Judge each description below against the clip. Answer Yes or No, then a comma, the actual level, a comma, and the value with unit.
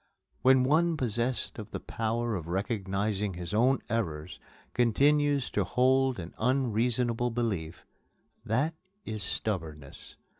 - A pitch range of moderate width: Yes, average, 4.7 semitones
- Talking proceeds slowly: Yes, slow, 115 wpm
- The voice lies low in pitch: Yes, low, 115 Hz